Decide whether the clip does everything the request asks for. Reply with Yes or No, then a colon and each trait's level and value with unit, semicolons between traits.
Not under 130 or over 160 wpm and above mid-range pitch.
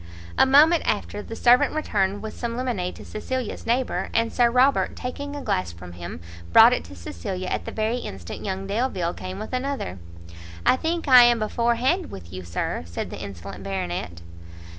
No: average, 185 wpm; high, 220 Hz